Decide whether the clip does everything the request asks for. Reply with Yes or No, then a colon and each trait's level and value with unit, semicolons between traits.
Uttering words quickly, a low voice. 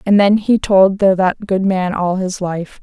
No: fast, 235 wpm; high, 190 Hz